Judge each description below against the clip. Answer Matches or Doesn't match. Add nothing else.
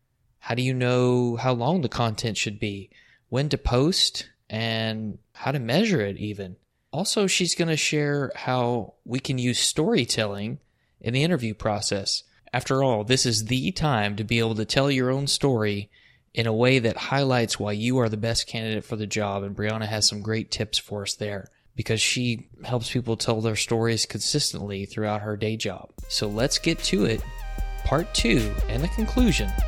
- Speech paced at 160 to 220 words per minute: Matches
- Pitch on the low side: Matches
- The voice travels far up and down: Doesn't match